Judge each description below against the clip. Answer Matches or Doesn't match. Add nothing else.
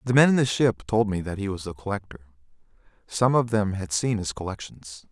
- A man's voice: Matches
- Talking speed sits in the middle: Doesn't match